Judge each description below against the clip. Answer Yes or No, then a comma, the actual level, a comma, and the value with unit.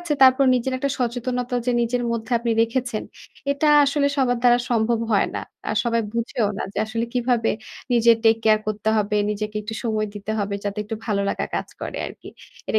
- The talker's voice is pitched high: Yes, high, 230 Hz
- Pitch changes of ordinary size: No, narrow, 2.3 semitones